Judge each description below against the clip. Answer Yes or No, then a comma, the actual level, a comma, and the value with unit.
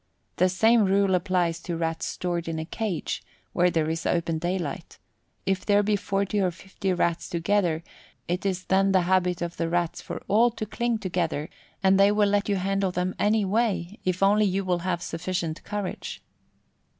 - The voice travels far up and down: No, narrow, 2.6 semitones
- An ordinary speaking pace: Yes, average, 180 wpm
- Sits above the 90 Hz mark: Yes, medium, 185 Hz